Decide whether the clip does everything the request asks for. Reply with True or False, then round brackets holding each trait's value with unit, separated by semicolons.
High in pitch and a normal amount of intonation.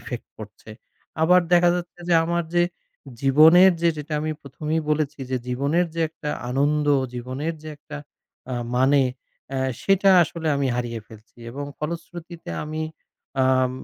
False (150 Hz; 4.2 semitones)